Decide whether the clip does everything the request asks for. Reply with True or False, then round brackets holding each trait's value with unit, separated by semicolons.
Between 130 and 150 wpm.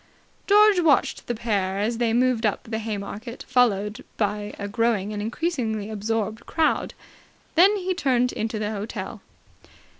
True (145 wpm)